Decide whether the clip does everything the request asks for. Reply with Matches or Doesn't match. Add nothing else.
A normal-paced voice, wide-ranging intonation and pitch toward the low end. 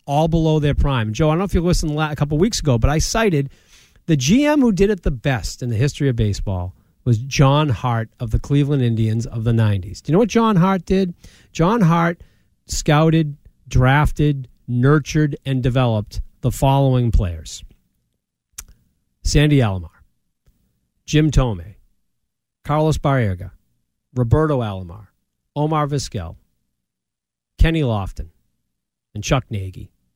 Matches